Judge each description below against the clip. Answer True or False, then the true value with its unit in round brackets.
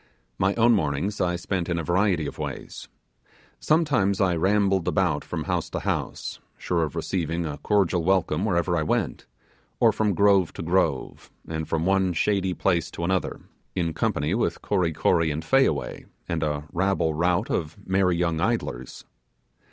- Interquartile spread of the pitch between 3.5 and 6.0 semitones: False (3.1 semitones)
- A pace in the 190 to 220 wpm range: False (165 wpm)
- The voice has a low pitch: True (90 Hz)